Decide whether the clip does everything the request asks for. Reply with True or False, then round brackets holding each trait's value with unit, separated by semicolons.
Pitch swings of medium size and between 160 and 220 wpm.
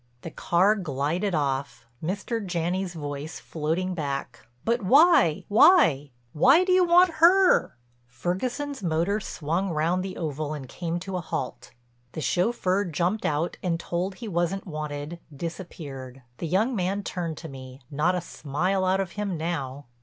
False (4.5 semitones; 150 wpm)